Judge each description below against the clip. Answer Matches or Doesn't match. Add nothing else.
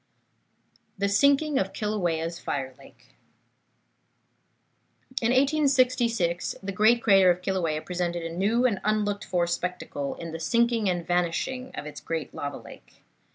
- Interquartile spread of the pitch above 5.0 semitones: Matches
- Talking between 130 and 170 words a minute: Matches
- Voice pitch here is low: Doesn't match